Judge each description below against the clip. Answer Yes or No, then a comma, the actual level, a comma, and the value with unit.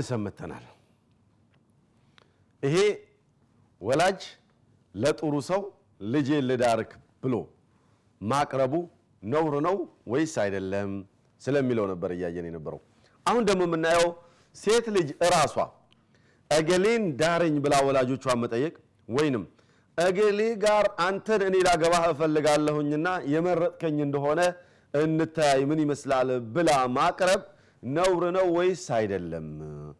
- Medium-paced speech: Yes, average, 90 wpm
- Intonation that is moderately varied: No, wide, 6.6 semitones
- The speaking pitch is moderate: Yes, medium, 150 Hz